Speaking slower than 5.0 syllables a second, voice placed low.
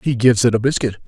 No: 6.8 syllables/s; low, 120 Hz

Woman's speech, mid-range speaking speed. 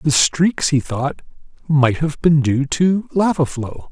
No: male; average, 170 wpm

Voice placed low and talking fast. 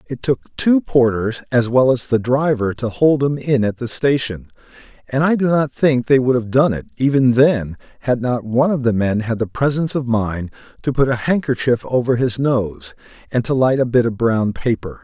Yes: low, 125 Hz; fast, 215 wpm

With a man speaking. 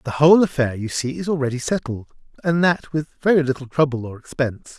Yes: male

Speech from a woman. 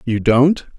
No: male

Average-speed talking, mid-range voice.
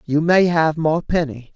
Yes: average, 195 wpm; medium, 160 Hz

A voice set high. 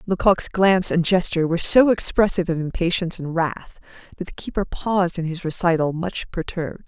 No: medium, 175 Hz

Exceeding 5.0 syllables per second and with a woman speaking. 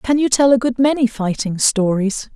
No: 4.8 syllables/s; female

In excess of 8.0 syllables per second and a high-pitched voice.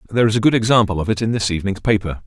No: 8.4 syllables/s; low, 105 Hz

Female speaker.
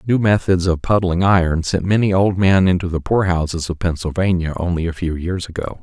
No: male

